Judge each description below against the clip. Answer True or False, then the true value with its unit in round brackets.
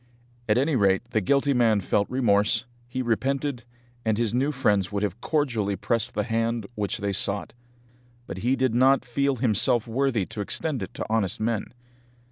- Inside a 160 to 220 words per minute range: True (175 wpm)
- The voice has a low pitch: True (115 Hz)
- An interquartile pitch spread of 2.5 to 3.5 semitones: False (3.9 semitones)